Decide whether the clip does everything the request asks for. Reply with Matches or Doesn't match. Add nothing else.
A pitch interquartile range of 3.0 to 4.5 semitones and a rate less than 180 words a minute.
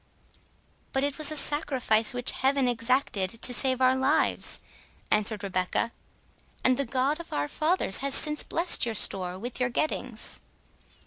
Matches